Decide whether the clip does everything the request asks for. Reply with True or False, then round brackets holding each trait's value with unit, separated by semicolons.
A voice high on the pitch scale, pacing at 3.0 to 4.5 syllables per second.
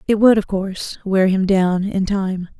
True (195 Hz; 4.4 syllables/s)